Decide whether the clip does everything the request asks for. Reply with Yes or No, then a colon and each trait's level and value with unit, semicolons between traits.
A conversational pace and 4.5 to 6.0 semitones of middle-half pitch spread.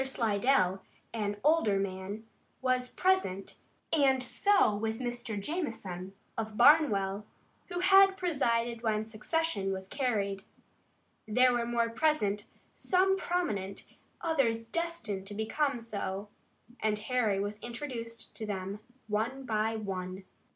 No: slow, 115 wpm; average, 5.0 semitones